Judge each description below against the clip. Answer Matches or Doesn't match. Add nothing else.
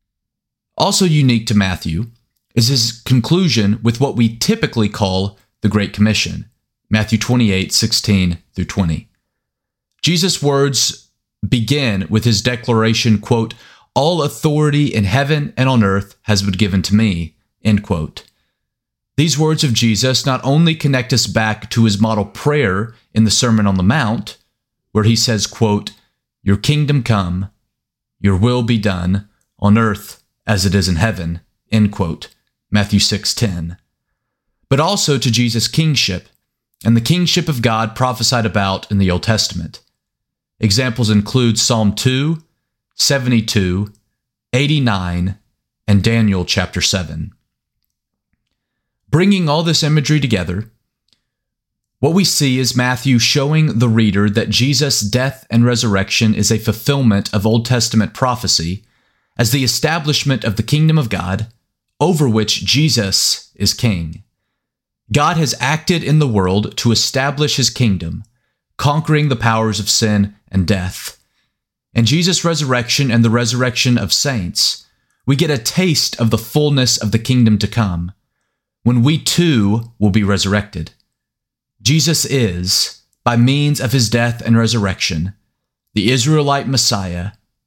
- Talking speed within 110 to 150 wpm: Matches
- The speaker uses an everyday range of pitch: Matches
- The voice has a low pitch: Matches